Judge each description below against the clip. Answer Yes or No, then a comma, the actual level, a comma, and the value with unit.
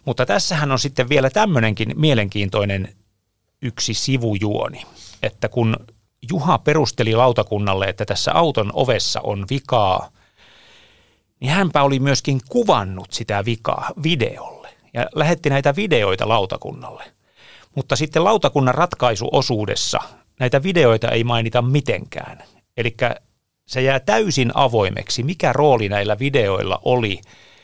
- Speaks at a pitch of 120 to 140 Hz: Yes, low, 125 Hz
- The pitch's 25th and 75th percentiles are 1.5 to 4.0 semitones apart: No, average, 5.1 semitones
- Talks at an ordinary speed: Yes, average, 115 wpm